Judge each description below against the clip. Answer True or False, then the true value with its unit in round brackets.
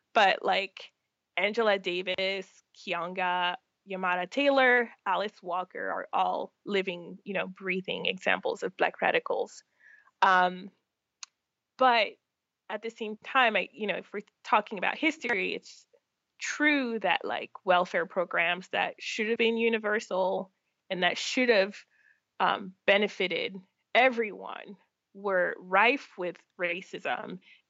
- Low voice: False (200 Hz)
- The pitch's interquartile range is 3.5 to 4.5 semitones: True (4.0 semitones)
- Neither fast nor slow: False (120 wpm)